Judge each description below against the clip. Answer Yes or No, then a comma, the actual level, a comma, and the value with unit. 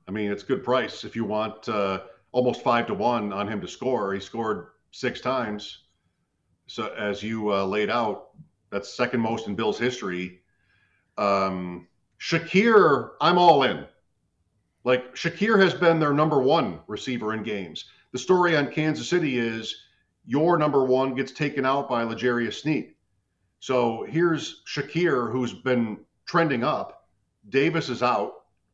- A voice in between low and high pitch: No, low, 120 Hz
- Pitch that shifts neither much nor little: No, wide, 5.9 semitones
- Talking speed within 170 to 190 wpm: No, average, 150 wpm